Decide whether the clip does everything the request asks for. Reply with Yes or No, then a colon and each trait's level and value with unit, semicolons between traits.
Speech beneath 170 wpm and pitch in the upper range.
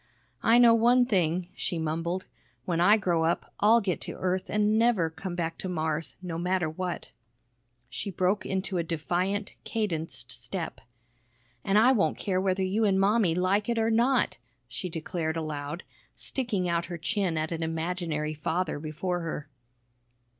No: average, 160 wpm; medium, 180 Hz